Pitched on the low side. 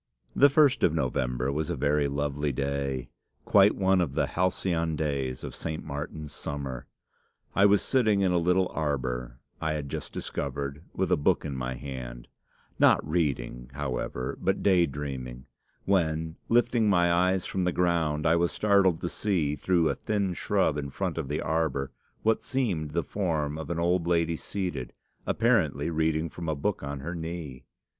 Yes: very low, 80 Hz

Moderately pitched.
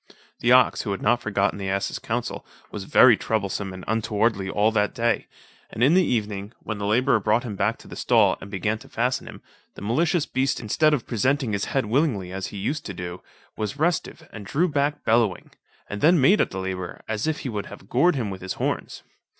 No: low, 110 Hz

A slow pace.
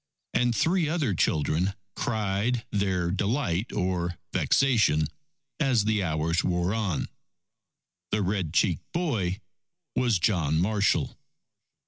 Yes: slow, 105 wpm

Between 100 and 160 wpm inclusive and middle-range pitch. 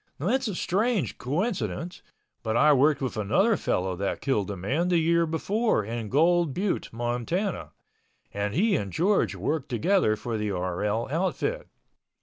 Yes: average, 150 wpm; medium, 150 Hz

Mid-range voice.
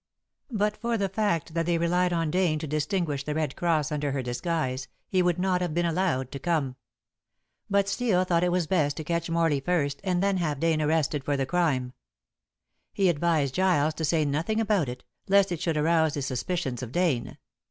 Yes: medium, 165 Hz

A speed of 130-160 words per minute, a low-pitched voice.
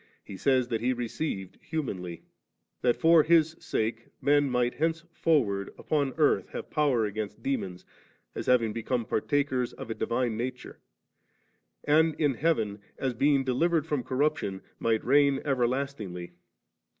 Yes: average, 140 wpm; low, 130 Hz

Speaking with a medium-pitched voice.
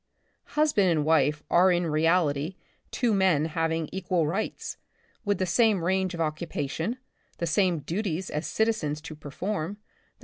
Yes: medium, 170 Hz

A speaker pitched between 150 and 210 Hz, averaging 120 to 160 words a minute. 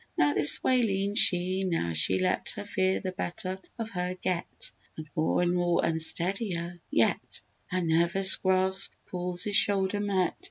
Yes: medium, 185 Hz; average, 155 wpm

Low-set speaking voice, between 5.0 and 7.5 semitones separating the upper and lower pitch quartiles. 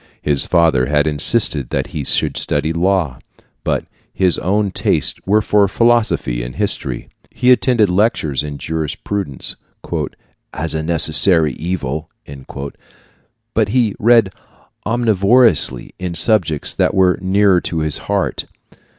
Yes: very low, 90 Hz; average, 5.3 semitones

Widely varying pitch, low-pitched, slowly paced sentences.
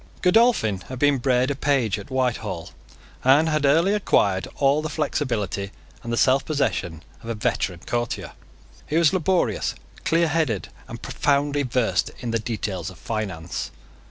No: wide, 5.8 semitones; low, 125 Hz; average, 145 wpm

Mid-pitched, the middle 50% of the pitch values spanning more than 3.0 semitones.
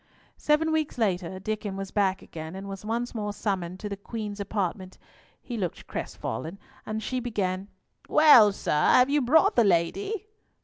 No: high, 205 Hz; average, 4.4 semitones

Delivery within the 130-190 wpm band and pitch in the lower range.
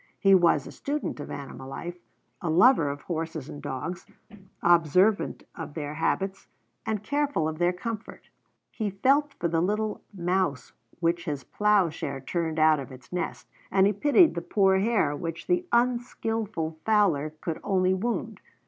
No: average, 155 wpm; medium, 180 Hz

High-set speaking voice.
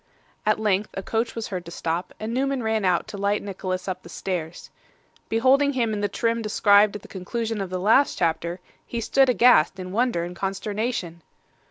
Yes: high, 205 Hz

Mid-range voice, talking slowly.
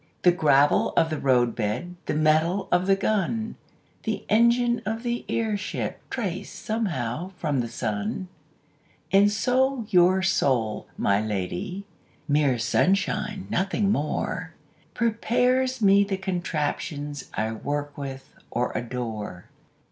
Yes: medium, 175 Hz; slow, 120 wpm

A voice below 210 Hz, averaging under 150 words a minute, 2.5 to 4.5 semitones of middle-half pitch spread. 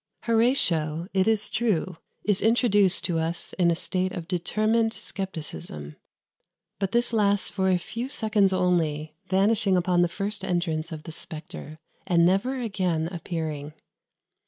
Yes: medium, 185 Hz; average, 140 wpm; average, 4.2 semitones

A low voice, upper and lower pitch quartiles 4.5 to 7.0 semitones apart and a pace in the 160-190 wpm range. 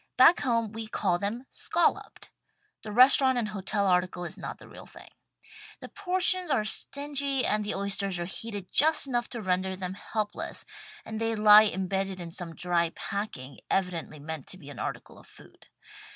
No: high, 205 Hz; average, 4.8 semitones; average, 175 wpm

